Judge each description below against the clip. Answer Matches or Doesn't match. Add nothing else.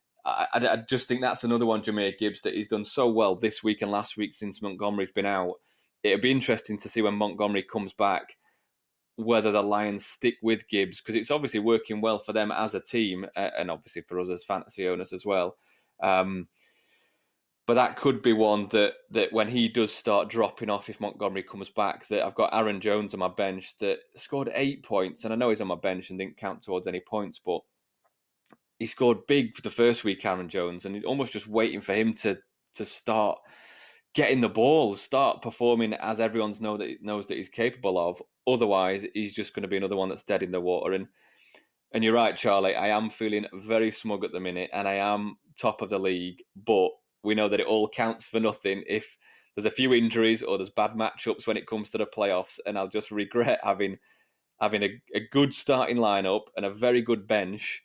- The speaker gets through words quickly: Matches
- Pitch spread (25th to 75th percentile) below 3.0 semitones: Matches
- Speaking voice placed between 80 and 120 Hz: Matches